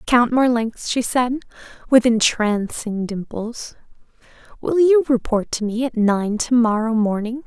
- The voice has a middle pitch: No, high, 235 Hz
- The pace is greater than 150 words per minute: No, slow, 135 wpm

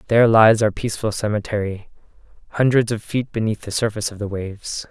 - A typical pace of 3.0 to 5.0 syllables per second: No, 6.2 syllables/s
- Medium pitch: No, low, 110 Hz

